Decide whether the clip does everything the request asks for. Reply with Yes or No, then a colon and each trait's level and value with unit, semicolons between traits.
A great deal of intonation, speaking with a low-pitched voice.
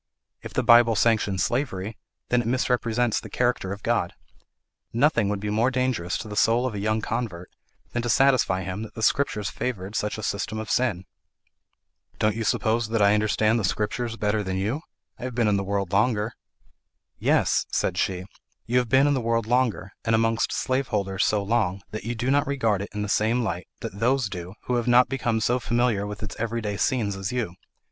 No: average, 3.0 semitones; low, 110 Hz